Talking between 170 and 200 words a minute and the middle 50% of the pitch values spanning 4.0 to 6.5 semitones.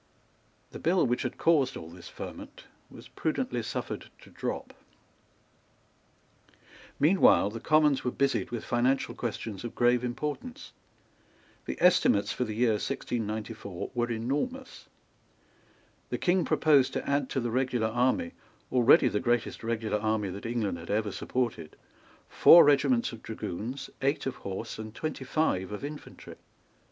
No: average, 140 wpm; average, 4.3 semitones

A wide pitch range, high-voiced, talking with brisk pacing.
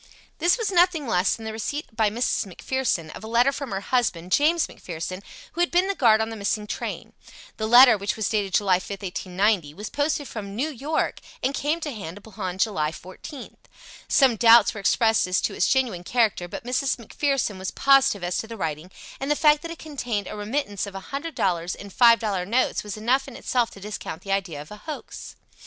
Yes: wide, 5.7 semitones; high, 220 Hz; fast, 215 wpm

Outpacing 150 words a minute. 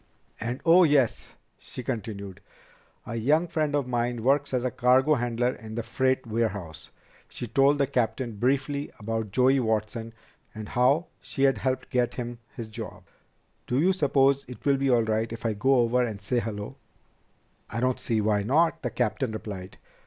Yes: average, 175 wpm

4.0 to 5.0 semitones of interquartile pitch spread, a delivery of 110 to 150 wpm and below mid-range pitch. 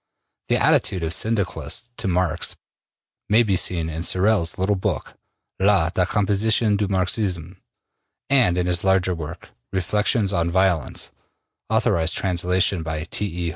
No: average, 3.1 semitones; slow, 135 wpm; very low, 95 Hz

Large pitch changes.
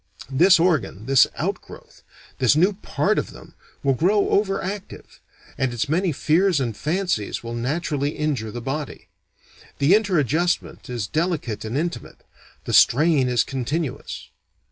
Yes: wide, 5.8 semitones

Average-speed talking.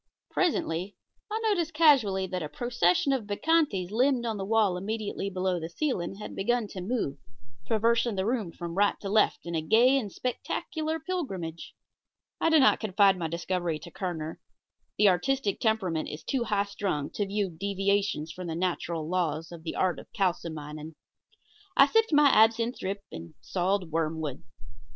Yes: average, 170 wpm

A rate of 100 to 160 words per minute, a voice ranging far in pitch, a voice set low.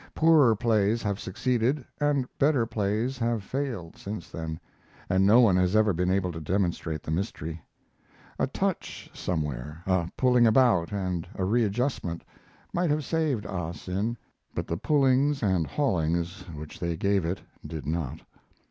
Yes: average, 150 wpm; wide, 6.2 semitones; low, 100 Hz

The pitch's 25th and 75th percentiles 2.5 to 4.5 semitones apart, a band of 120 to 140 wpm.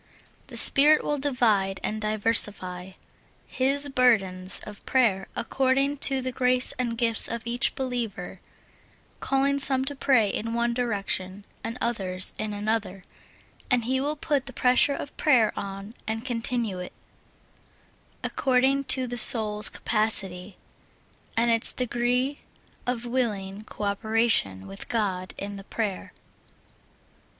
Yes: average, 4.2 semitones; slow, 135 wpm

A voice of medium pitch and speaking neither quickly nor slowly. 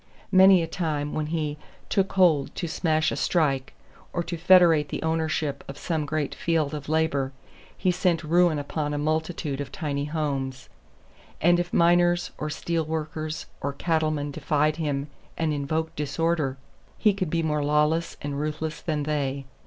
Yes: medium, 155 Hz; average, 160 wpm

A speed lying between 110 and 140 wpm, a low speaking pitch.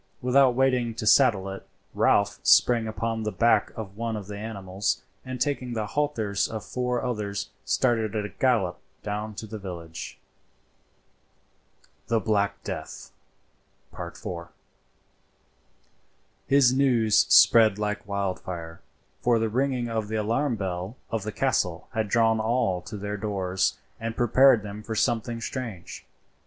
Yes: slow, 135 wpm; low, 110 Hz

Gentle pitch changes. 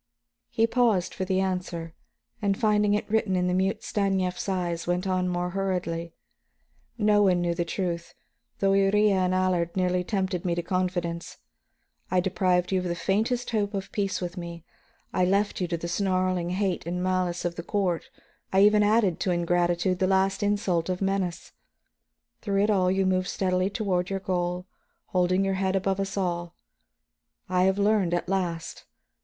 Yes: narrow, 1.8 semitones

